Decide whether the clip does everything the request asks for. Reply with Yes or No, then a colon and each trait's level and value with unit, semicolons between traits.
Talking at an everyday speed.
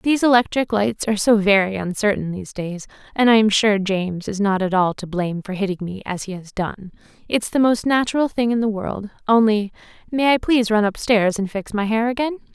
No: fast, 220 wpm